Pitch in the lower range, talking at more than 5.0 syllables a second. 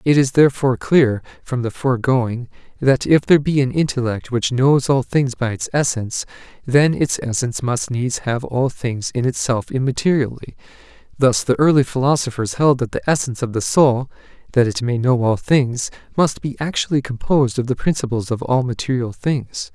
Yes: low, 130 Hz; 5.2 syllables/s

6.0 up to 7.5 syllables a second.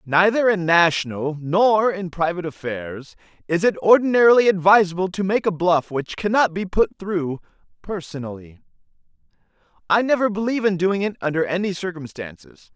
No: 5.2 syllables/s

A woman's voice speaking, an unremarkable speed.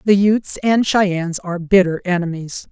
Yes: female; average, 155 wpm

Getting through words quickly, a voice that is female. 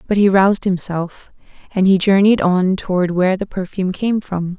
No: average, 185 wpm; female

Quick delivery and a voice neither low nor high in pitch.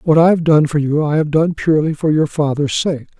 Yes: fast, 265 wpm; medium, 155 Hz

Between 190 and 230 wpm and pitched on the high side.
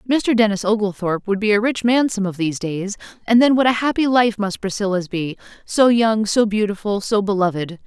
Yes: average, 200 wpm; high, 210 Hz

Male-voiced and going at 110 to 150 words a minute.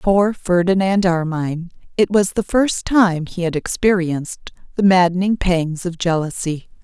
No: female; average, 140 wpm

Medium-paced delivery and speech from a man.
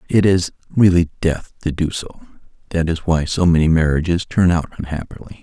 Yes: average, 165 wpm; male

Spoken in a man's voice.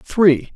Yes: male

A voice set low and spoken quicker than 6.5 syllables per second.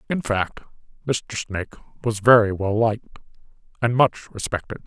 No: low, 110 Hz; 4.8 syllables/s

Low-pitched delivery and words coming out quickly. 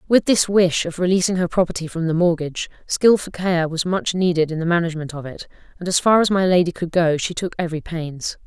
No: medium, 175 Hz; fast, 225 wpm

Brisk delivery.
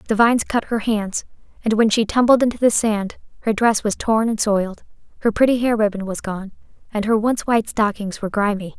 Yes: fast, 210 wpm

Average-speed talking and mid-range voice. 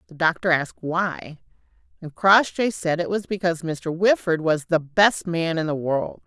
Yes: average, 180 wpm; medium, 170 Hz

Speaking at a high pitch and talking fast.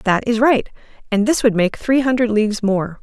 Yes: high, 225 Hz; fast, 220 wpm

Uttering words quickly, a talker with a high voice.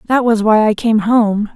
Yes: fast, 230 wpm; high, 220 Hz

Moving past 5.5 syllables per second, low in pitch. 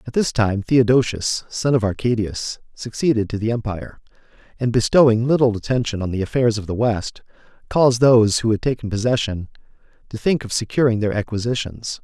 Yes: 5.7 syllables/s; low, 115 Hz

